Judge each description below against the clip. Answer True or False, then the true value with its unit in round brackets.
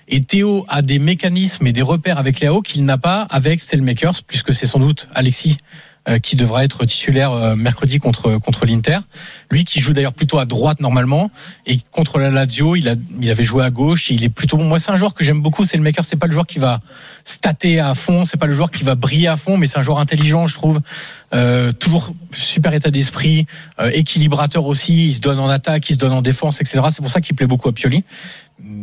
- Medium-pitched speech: True (150 Hz)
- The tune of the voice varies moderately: True (3.7 semitones)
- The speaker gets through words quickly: True (235 wpm)